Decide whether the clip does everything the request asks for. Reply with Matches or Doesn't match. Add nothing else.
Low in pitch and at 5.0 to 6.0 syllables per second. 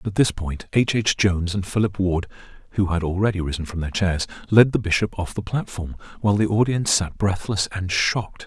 Matches